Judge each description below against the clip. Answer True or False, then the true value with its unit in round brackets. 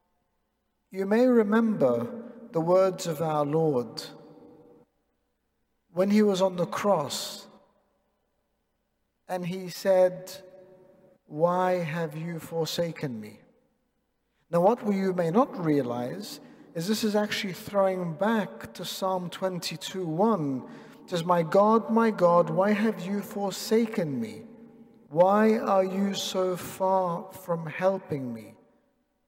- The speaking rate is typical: False (115 wpm)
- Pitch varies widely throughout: False (3.2 semitones)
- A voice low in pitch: False (190 Hz)